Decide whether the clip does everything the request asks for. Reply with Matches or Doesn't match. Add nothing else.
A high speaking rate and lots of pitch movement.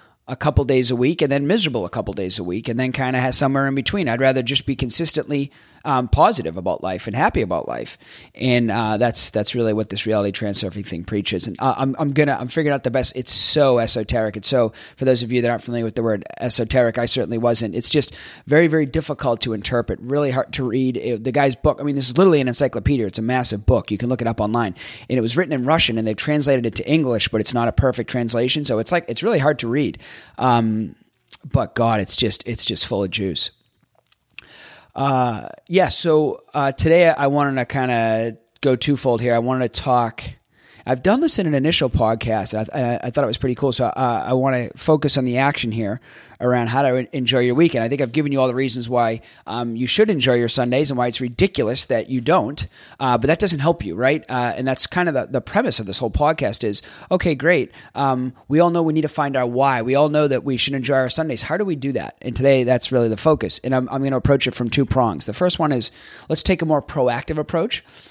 Doesn't match